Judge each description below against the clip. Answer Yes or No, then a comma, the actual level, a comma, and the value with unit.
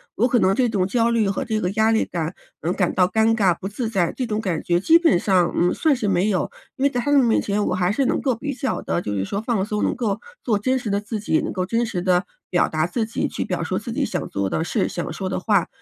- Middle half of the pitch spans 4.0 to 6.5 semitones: Yes, average, 4.5 semitones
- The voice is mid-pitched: No, high, 210 Hz